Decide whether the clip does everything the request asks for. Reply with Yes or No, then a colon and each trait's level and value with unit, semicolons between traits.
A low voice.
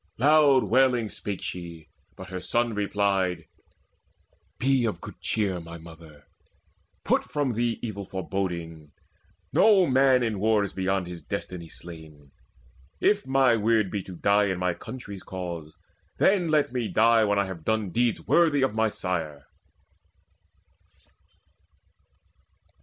Yes: low, 100 Hz